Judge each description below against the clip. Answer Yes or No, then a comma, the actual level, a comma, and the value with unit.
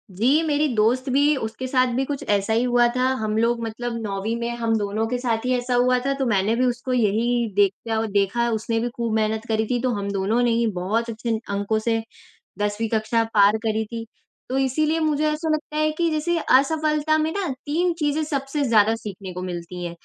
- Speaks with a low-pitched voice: No, high, 235 Hz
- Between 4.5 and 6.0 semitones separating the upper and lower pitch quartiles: No, average, 3.7 semitones